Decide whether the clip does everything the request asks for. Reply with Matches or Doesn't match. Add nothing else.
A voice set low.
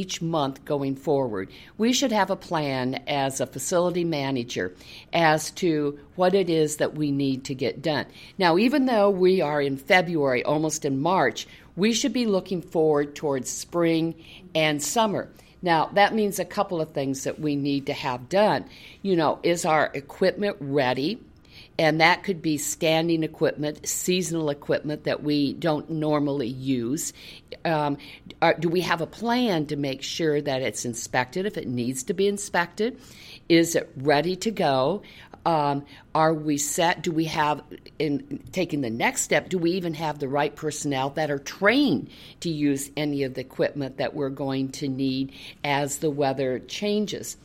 Doesn't match